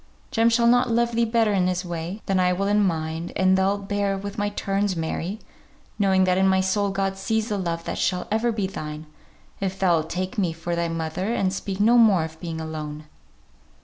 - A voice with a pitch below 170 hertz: No, high, 190 Hz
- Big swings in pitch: No, average, 3.2 semitones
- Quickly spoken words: Yes, fast, 215 wpm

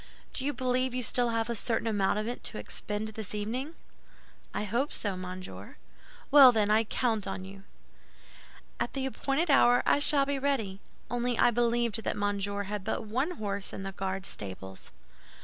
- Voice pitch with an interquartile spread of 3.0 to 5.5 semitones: Yes, average, 3.9 semitones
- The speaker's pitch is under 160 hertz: No, high, 225 Hz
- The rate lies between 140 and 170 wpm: No, average, 180 wpm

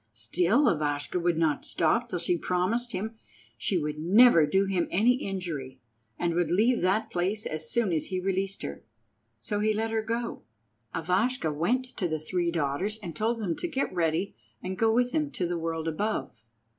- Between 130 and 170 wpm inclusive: No, average, 185 wpm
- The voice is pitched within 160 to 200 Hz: Yes, medium, 185 Hz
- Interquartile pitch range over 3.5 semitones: Yes, average, 5.1 semitones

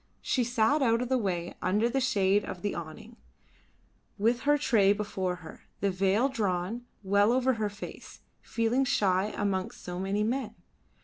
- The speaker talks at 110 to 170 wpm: Yes, average, 165 wpm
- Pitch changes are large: No, average, 4.0 semitones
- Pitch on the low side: No, high, 210 Hz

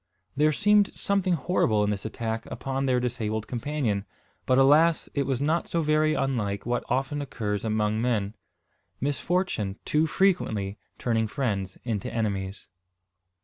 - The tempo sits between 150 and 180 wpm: No, average, 140 wpm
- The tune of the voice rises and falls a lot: Yes, wide, 5.9 semitones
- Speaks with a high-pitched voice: No, low, 125 Hz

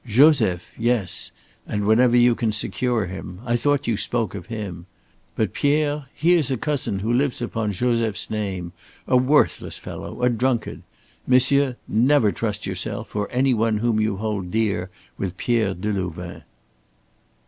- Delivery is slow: No, average, 150 wpm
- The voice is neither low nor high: No, low, 115 Hz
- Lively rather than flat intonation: No, average, 3.8 semitones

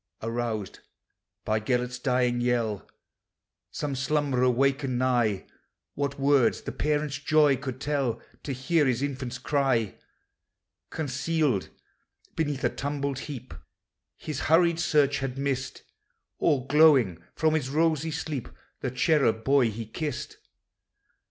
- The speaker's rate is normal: No, slow, 120 wpm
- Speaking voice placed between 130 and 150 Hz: Yes, low, 135 Hz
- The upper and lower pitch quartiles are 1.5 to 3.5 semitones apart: Yes, average, 3.0 semitones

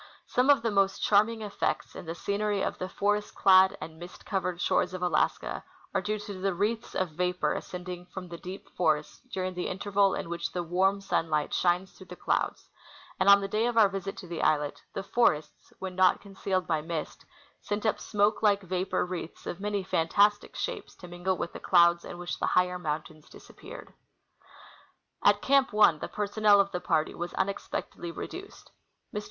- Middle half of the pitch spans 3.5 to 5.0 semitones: No, narrow, 2.6 semitones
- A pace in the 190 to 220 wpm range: Yes, average, 195 wpm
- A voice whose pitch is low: No, medium, 185 Hz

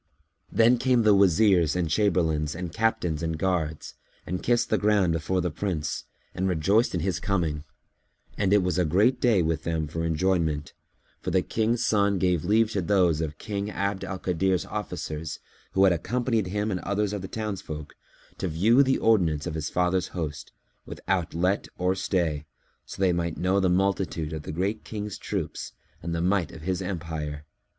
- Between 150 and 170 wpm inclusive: No, average, 180 wpm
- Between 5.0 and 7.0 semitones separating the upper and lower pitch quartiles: No, average, 3.8 semitones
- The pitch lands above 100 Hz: No, very low, 90 Hz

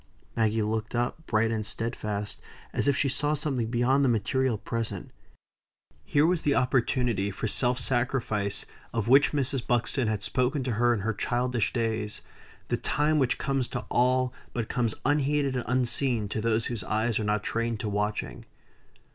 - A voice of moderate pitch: No, low, 120 Hz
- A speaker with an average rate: Yes, average, 170 wpm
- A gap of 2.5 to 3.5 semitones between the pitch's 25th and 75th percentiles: Yes, average, 3.2 semitones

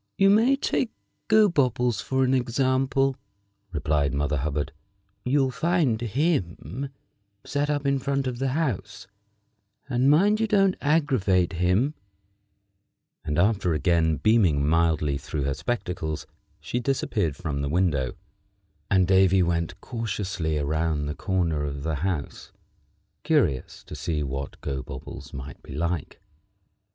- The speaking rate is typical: No, slow, 125 wpm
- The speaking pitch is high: No, very low, 95 Hz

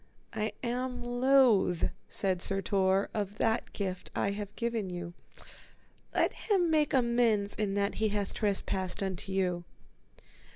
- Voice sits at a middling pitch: No, high, 205 Hz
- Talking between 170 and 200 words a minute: No, slow, 135 wpm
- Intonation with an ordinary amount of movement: Yes, average, 3.6 semitones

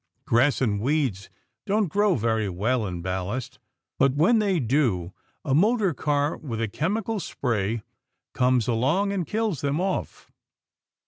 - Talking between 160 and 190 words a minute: No, average, 140 wpm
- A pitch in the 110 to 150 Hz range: Yes, low, 135 Hz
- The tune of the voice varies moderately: No, wide, 8.2 semitones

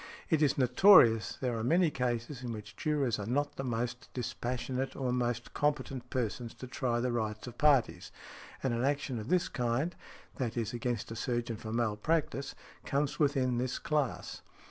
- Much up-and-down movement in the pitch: No, average, 2.9 semitones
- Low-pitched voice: Yes, low, 125 Hz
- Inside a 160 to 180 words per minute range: Yes, average, 170 wpm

